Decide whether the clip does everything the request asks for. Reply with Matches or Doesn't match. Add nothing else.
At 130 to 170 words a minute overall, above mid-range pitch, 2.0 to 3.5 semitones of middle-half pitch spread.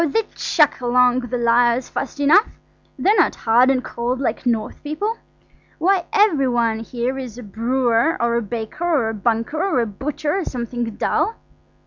Doesn't match